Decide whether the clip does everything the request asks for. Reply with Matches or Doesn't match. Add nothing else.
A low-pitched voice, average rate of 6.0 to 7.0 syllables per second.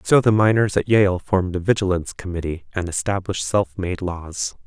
Doesn't match